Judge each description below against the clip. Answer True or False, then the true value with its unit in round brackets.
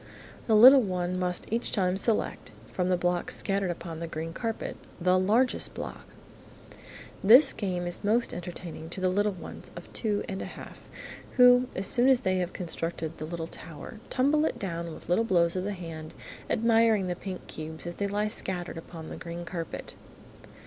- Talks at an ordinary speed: True (185 wpm)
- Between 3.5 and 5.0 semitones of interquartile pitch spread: True (3.8 semitones)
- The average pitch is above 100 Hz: True (185 Hz)